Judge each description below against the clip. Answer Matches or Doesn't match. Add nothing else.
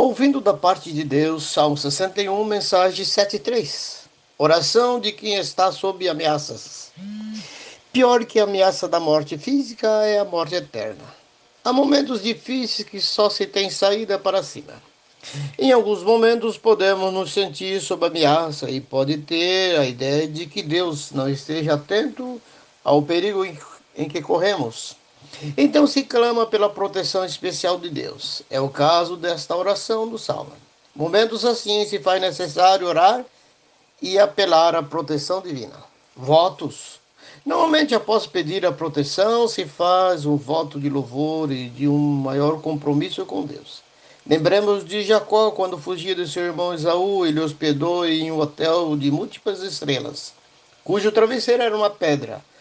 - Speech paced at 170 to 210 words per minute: Doesn't match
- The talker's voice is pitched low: Doesn't match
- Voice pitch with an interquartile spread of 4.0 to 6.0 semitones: Matches